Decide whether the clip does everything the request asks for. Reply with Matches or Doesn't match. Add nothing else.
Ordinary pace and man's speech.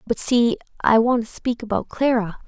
Doesn't match